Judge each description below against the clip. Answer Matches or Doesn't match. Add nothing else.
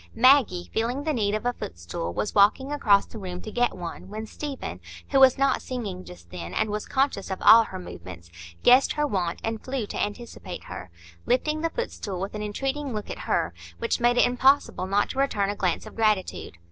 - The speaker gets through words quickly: Matches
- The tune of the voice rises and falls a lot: Matches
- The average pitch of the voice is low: Doesn't match